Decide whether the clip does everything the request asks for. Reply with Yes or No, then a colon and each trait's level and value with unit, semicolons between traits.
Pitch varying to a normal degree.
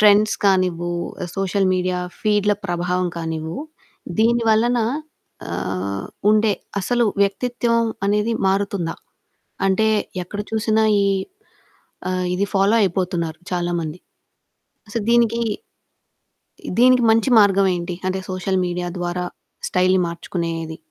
Yes: average, 3.6 semitones